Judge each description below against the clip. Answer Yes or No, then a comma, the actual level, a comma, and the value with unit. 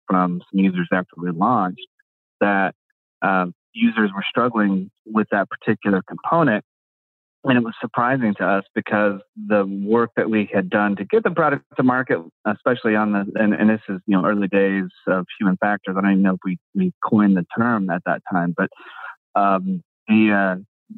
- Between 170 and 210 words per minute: Yes, average, 185 wpm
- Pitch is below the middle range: Yes, low, 105 Hz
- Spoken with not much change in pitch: No, average, 3.2 semitones